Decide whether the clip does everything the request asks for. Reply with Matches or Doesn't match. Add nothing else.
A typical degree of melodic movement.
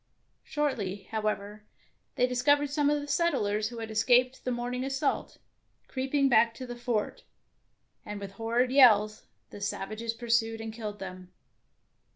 Matches